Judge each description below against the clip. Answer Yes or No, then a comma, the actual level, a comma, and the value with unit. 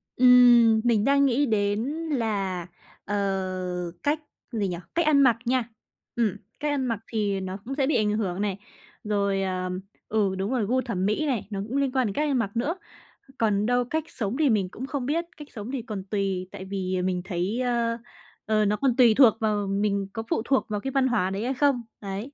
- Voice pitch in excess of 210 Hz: Yes, high, 220 Hz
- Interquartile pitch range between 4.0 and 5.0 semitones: Yes, average, 4.4 semitones